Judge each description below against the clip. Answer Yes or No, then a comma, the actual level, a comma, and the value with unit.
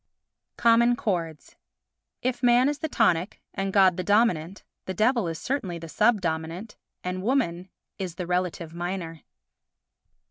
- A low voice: No, medium, 185 Hz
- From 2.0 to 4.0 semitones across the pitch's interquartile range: No, average, 5.2 semitones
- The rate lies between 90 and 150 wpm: Yes, average, 140 wpm